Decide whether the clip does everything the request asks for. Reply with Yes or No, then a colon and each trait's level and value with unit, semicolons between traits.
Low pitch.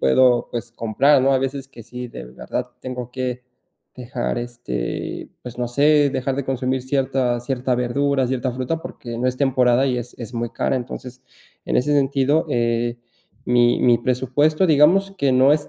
Yes: low, 130 Hz